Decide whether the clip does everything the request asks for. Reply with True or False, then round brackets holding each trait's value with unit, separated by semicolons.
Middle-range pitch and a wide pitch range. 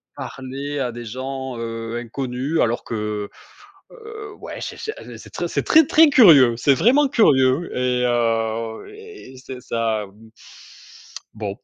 False (130 Hz; 5.8 semitones)